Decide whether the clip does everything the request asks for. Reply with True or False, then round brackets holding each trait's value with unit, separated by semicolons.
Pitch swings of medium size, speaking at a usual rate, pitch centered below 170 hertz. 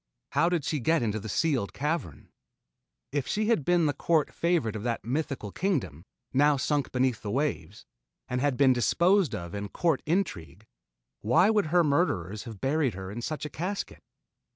False (7.2 semitones; 175 wpm; 140 Hz)